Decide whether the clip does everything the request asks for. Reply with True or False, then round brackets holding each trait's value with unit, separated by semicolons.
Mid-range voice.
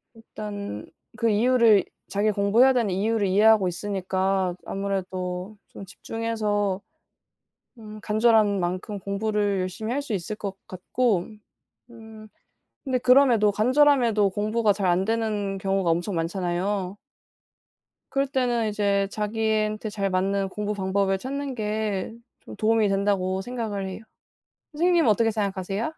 False (210 Hz)